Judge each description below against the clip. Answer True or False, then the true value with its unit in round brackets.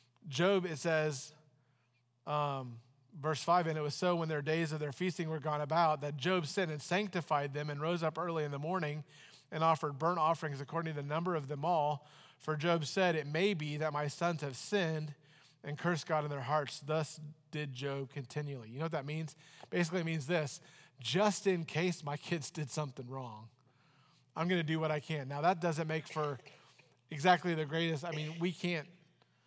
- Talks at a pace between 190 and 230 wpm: True (205 wpm)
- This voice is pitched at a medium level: True (155 Hz)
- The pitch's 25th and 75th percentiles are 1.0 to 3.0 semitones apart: True (2.4 semitones)